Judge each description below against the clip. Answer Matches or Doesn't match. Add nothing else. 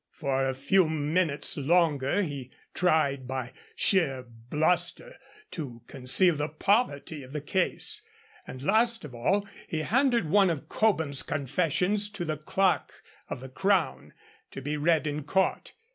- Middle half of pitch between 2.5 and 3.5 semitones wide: Doesn't match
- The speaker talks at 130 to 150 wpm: Matches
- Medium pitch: Matches